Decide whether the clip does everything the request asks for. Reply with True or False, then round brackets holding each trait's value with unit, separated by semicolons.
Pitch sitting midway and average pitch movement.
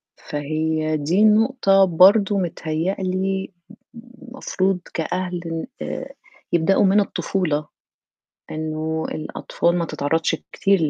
True (180 Hz; 3.5 semitones)